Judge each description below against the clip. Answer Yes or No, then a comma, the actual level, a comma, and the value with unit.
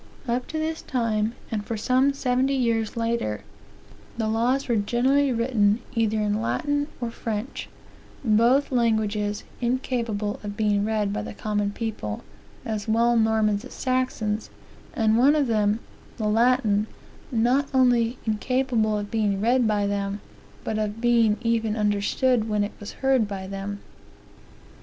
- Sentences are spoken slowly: No, average, 145 wpm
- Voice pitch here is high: Yes, high, 225 Hz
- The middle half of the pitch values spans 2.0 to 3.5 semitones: Yes, average, 2.9 semitones